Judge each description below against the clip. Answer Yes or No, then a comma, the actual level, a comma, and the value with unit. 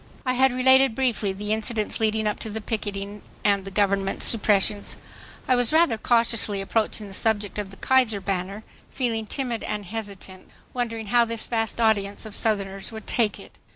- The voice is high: Yes, high, 215 Hz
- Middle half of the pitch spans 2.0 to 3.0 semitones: Yes, narrow, 2.5 semitones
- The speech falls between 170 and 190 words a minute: Yes, average, 175 wpm